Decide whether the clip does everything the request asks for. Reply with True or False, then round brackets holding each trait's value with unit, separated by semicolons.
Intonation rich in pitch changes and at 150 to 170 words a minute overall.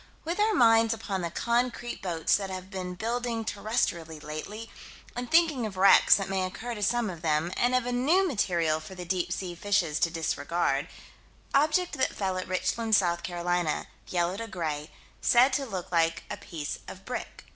False (5.7 semitones; 185 wpm)